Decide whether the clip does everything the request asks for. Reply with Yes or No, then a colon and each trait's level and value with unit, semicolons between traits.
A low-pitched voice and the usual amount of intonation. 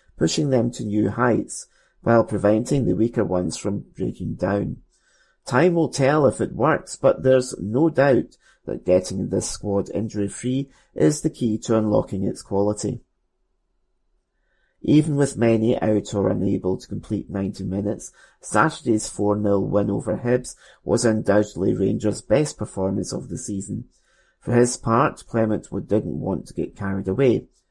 Yes: low, 105 Hz; average, 3.6 semitones